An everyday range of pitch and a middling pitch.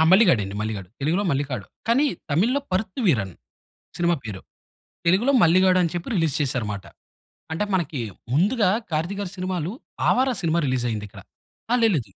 No: wide, 7.1 semitones; medium, 170 Hz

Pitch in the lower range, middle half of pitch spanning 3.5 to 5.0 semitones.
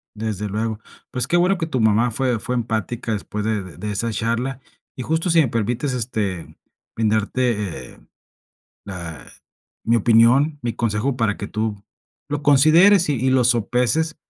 Yes: low, 115 Hz; average, 3.8 semitones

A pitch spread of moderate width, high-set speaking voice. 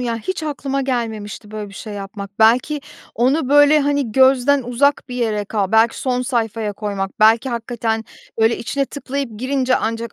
Yes: average, 3.6 semitones; high, 235 Hz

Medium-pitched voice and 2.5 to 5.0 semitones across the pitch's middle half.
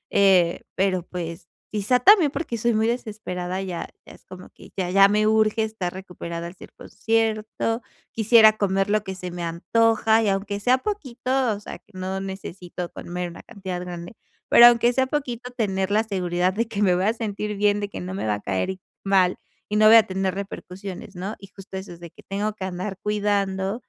No: high, 200 Hz; average, 3.1 semitones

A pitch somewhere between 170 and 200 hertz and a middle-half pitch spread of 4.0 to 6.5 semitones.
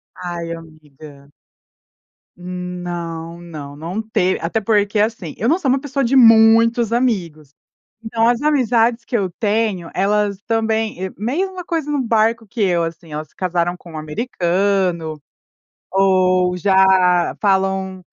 Yes: high, 190 Hz; average, 4.7 semitones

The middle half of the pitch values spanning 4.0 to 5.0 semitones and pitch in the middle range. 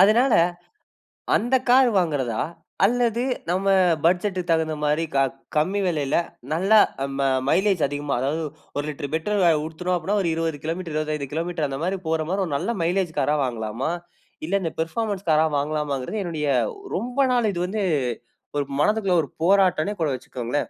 Yes: average, 4.6 semitones; medium, 165 Hz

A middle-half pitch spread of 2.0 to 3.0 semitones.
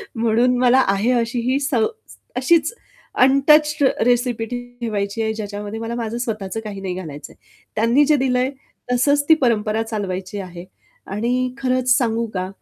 No: average, 3.4 semitones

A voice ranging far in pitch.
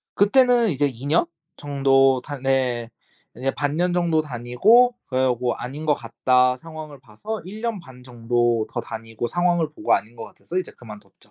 Yes: wide, 5.9 semitones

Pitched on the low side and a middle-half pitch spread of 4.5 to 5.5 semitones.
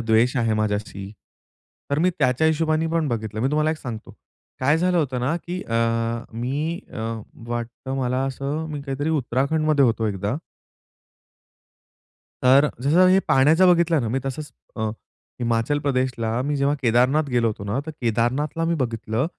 Yes: low, 130 Hz; average, 4.9 semitones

